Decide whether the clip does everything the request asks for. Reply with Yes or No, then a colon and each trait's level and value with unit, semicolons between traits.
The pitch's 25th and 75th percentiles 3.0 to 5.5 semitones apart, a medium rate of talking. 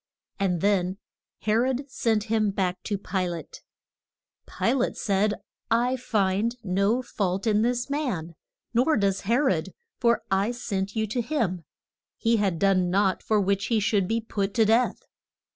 Yes: average, 3.4 semitones; average, 160 wpm